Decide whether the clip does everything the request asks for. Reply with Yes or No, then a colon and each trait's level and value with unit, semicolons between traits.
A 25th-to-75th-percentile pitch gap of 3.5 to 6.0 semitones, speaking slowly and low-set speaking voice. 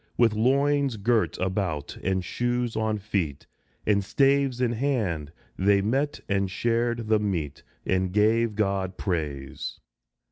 Yes: average, 4.2 semitones; slow, 130 wpm; low, 105 Hz